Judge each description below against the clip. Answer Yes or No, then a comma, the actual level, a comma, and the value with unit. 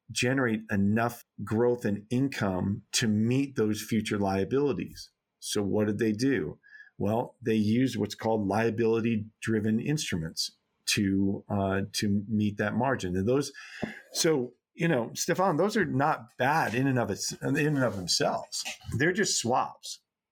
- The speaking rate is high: No, average, 145 wpm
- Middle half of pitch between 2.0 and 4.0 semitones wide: Yes, average, 2.9 semitones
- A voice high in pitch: No, low, 110 Hz